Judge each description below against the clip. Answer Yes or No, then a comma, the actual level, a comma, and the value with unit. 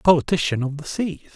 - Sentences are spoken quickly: Yes, fast, 220 wpm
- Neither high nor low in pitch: Yes, medium, 155 Hz